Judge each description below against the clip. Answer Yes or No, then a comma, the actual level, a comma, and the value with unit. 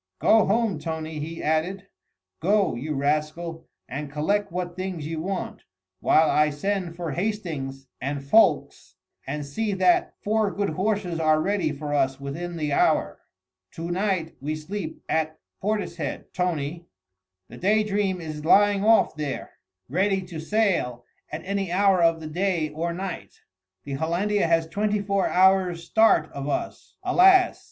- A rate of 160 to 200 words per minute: No, average, 150 wpm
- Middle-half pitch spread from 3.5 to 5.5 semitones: Yes, average, 4.4 semitones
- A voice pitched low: No, medium, 170 Hz